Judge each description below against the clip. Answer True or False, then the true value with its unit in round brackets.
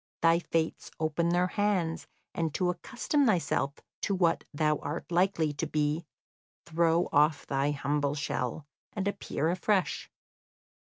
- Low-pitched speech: False (165 Hz)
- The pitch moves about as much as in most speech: True (3.1 semitones)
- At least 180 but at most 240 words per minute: False (135 wpm)